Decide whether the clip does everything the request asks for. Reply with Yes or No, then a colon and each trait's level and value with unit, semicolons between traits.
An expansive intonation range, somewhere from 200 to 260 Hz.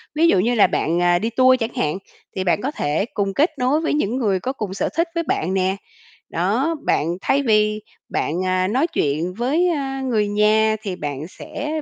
Yes: wide, 6.5 semitones; high, 215 Hz